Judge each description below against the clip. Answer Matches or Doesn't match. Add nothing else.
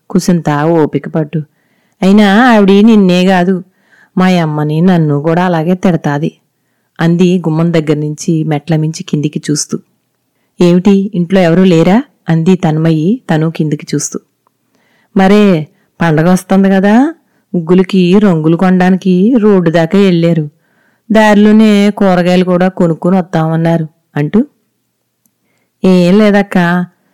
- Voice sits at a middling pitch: Matches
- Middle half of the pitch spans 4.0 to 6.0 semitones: Doesn't match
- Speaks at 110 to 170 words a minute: Doesn't match